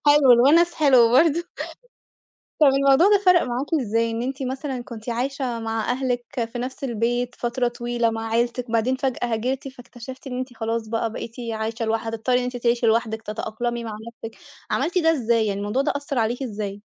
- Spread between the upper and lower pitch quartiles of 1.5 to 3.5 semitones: Yes, average, 2.7 semitones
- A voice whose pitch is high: Yes, high, 240 Hz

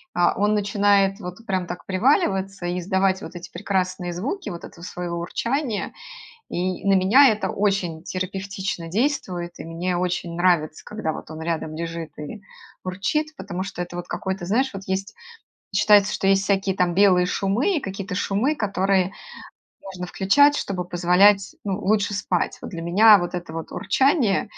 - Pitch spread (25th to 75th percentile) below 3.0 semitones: Yes, narrow, 2.5 semitones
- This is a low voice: No, high, 190 Hz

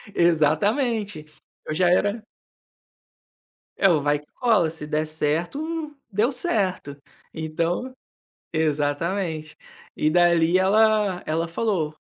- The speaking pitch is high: No, medium, 170 Hz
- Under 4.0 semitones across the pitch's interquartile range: No, average, 4.8 semitones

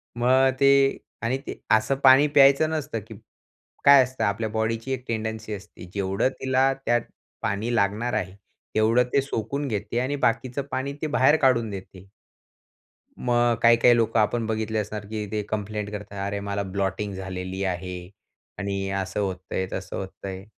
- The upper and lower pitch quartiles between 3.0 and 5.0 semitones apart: Yes, average, 3.9 semitones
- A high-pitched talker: No, low, 110 Hz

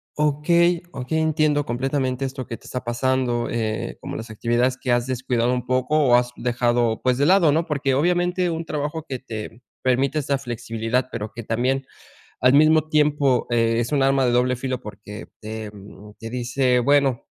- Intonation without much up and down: No, average, 3.4 semitones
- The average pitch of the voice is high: No, low, 130 Hz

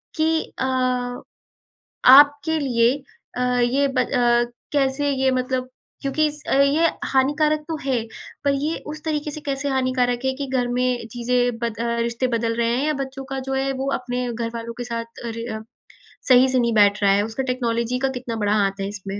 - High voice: Yes, very high, 255 Hz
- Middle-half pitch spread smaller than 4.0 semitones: Yes, average, 2.8 semitones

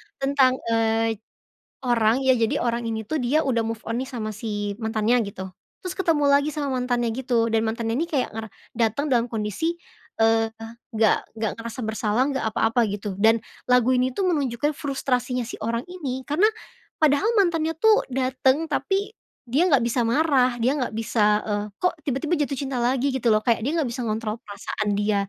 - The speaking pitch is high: Yes, high, 245 Hz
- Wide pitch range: No, average, 4.0 semitones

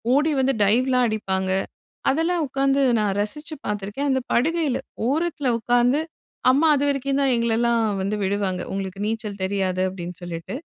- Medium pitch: No, high, 240 Hz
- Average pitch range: No, wide, 5.7 semitones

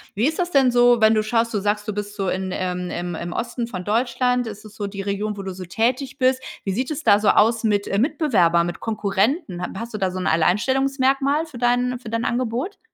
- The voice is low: No, high, 220 Hz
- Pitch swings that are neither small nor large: Yes, average, 4.1 semitones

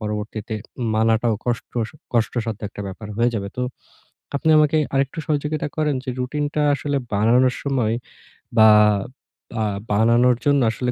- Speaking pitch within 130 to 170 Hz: No, low, 120 Hz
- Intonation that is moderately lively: Yes, average, 4.3 semitones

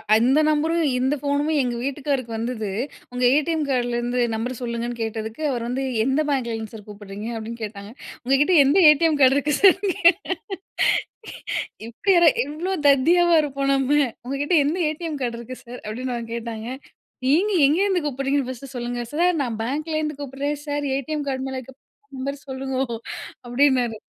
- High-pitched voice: Yes, very high, 265 Hz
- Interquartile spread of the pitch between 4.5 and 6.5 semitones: No, average, 3.7 semitones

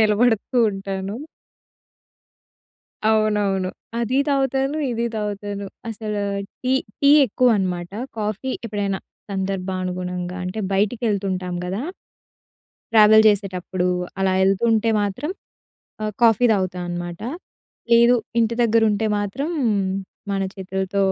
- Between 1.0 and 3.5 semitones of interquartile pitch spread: Yes, average, 2.9 semitones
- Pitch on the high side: Yes, high, 205 Hz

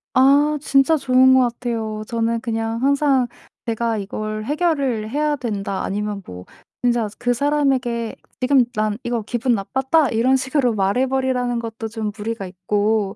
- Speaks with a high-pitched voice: Yes, high, 235 Hz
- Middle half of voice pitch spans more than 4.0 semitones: No, average, 3.6 semitones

